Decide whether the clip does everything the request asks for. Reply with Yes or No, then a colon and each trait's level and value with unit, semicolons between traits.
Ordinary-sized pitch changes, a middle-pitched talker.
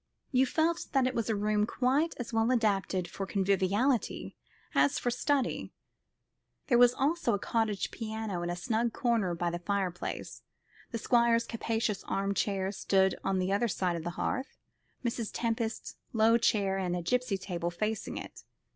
No: average, 3.8 semitones; high, 220 Hz